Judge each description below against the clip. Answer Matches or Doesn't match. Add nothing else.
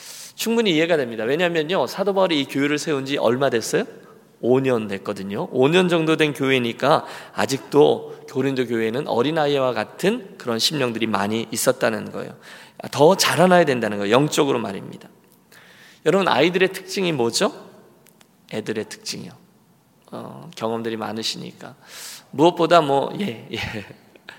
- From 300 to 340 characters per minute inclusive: Matches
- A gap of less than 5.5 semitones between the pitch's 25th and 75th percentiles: Doesn't match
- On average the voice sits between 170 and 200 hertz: Doesn't match